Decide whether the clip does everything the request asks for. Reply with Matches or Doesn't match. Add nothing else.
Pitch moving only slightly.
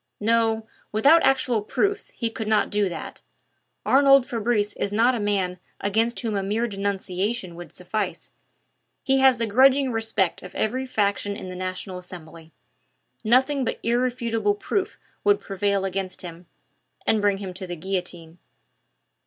Doesn't match